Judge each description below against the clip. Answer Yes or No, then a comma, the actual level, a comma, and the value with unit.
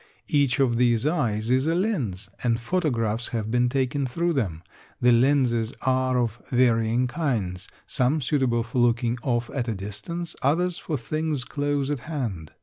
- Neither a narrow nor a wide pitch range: Yes, average, 3.8 semitones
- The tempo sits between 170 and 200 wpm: No, average, 160 wpm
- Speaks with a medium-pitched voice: No, low, 125 Hz